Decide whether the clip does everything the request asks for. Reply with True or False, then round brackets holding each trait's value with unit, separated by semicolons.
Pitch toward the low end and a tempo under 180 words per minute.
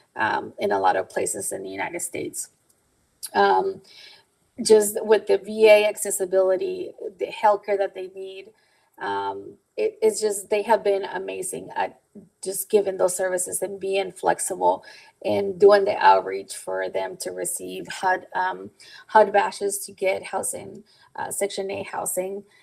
False (200 Hz; 150 wpm)